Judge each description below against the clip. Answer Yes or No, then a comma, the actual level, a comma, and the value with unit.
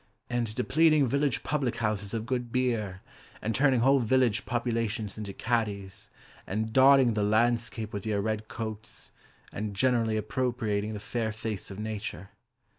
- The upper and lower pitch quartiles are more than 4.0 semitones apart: No, average, 2.7 semitones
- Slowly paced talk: No, average, 145 wpm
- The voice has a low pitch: Yes, low, 110 Hz